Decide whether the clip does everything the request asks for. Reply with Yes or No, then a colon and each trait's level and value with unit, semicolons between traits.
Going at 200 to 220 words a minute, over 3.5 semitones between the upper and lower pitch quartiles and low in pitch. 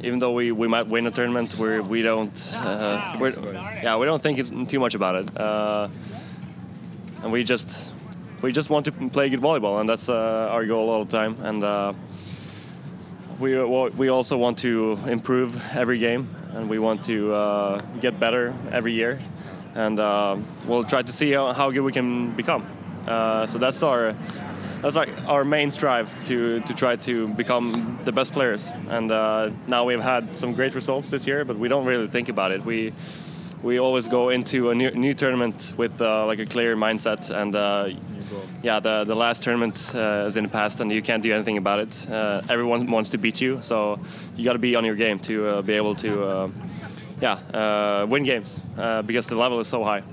No: fast, 205 wpm; average, 2.7 semitones; low, 115 Hz